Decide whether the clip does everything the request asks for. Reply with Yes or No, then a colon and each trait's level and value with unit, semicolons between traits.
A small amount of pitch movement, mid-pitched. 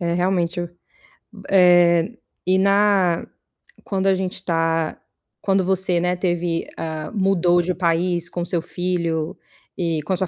Yes: narrow, 1.9 semitones; medium, 175 Hz